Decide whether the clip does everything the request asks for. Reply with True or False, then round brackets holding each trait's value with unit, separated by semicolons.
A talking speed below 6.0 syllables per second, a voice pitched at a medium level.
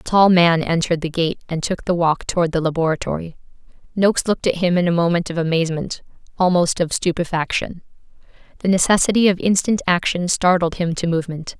False (6.1 syllables/s; 175 Hz)